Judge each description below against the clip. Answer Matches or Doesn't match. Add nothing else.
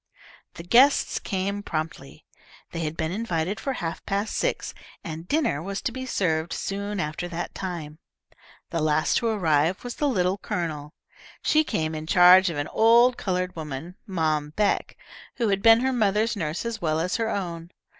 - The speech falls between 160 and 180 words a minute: Matches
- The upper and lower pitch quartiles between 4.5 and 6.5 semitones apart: Matches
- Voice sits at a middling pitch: Matches